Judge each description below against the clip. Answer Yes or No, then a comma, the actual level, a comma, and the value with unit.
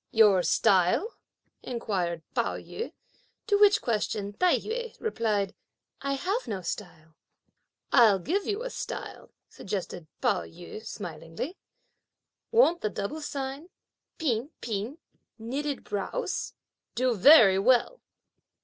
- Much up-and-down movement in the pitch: Yes, wide, 8.3 semitones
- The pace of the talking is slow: Yes, slow, 115 wpm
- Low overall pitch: No, high, 230 Hz